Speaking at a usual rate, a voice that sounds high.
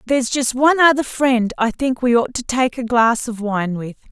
No: fast, 235 wpm; high, 245 Hz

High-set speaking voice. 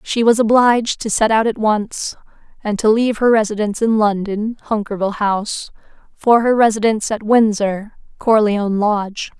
Yes: high, 215 Hz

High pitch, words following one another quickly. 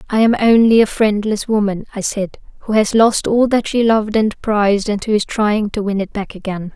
Yes: high, 210 Hz; fast, 230 wpm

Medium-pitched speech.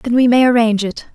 No: high, 235 Hz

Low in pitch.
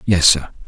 Yes: very low, 90 Hz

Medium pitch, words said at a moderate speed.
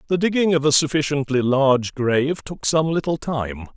Yes: medium, 145 Hz; average, 175 wpm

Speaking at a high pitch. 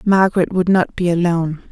No: medium, 175 Hz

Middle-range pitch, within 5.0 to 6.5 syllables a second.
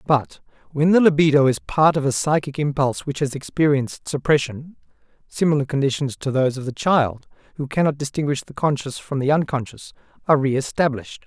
Yes: medium, 145 Hz; 5.8 syllables/s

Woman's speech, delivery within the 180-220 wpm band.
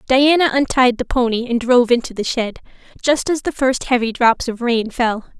Yes: female; average, 200 wpm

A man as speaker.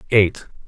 Yes: male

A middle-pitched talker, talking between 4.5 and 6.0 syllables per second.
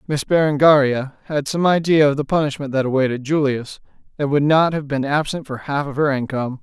Yes: medium, 145 Hz; 5.7 syllables/s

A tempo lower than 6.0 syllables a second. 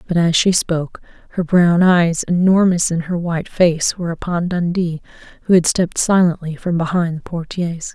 Yes: 5.2 syllables/s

